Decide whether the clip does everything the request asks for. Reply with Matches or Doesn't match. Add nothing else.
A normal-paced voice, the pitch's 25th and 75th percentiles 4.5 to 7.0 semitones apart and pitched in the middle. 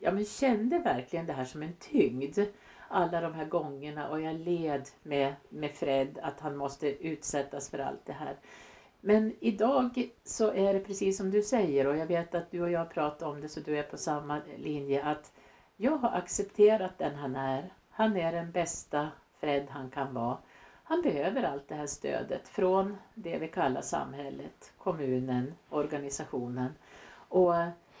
Matches